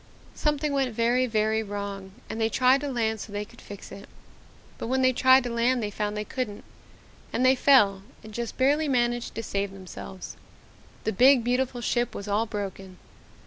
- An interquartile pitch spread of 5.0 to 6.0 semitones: No, average, 3.9 semitones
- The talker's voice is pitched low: No, high, 230 Hz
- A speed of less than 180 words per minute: No, average, 185 wpm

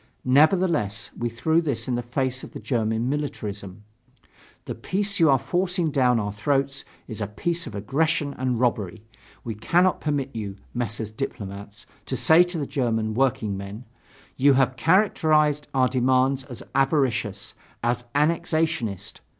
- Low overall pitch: Yes, low, 130 Hz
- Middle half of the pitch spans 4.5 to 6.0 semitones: Yes, average, 5.2 semitones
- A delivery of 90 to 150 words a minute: Yes, average, 145 wpm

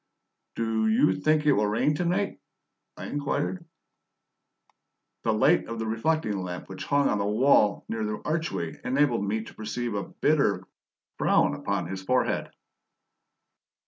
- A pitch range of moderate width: No, wide, 5.9 semitones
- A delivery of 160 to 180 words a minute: No, average, 145 wpm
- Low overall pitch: Yes, low, 115 Hz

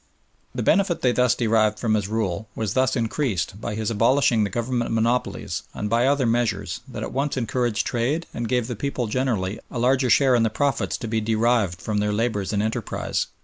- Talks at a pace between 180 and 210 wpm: Yes, average, 195 wpm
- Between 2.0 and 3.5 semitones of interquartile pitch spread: Yes, average, 2.7 semitones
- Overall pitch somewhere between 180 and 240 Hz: No, low, 115 Hz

